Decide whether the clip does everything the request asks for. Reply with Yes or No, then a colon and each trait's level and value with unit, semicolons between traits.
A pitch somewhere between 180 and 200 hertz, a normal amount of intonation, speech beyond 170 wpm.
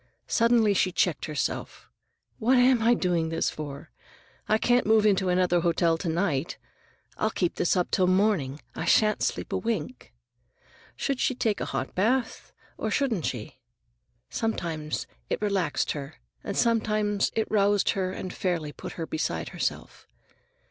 No: high, 190 Hz; average, 4.9 semitones; average, 155 wpm